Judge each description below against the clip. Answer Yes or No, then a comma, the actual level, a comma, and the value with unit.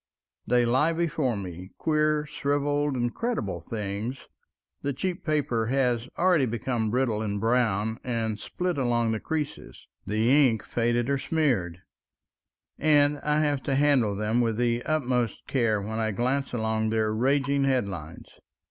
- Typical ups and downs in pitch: Yes, average, 4.6 semitones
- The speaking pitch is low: Yes, low, 120 Hz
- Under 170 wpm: Yes, average, 140 wpm